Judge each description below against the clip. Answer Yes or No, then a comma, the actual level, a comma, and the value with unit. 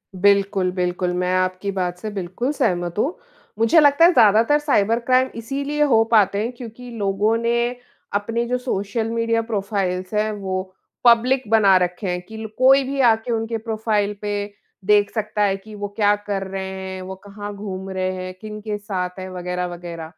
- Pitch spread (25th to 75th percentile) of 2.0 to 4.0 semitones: Yes, average, 3.4 semitones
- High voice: Yes, high, 205 Hz